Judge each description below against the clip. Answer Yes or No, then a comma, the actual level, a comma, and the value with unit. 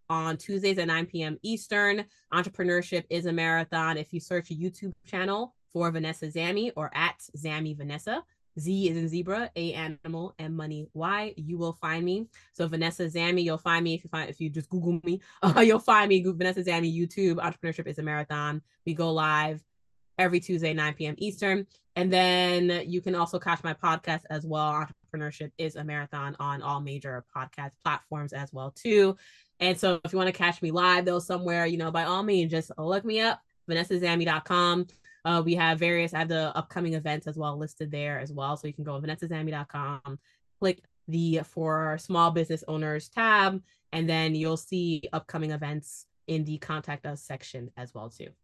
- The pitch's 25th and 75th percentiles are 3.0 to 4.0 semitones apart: No, narrow, 2.5 semitones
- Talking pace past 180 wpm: Yes, average, 190 wpm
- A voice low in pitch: No, medium, 165 Hz